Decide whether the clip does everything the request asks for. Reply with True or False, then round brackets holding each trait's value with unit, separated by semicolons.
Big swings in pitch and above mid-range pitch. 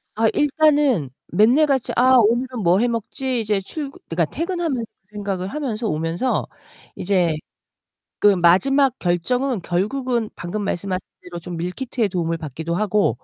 True (6.6 semitones; 210 Hz)